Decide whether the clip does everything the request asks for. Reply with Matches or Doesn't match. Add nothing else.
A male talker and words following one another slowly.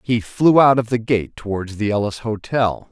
Doesn't match